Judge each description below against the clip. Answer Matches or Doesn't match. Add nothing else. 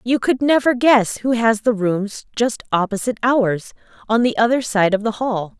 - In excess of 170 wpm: Matches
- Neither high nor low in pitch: Doesn't match